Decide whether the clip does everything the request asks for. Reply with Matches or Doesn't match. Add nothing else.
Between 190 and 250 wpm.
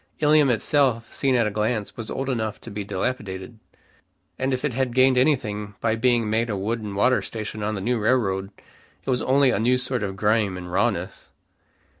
Matches